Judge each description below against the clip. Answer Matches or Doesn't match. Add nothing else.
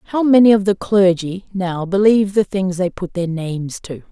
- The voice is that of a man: Doesn't match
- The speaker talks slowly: Doesn't match